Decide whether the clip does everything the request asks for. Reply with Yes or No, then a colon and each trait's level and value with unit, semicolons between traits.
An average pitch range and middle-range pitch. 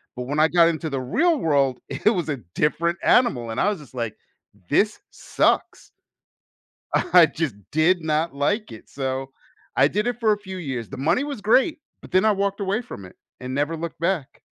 No: wide, 6.7 semitones; medium, 160 Hz